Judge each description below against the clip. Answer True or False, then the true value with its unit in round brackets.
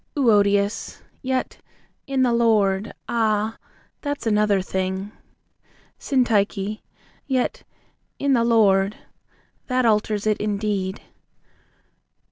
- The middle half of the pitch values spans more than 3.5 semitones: False (2.9 semitones)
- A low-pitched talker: False (215 Hz)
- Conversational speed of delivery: False (95 wpm)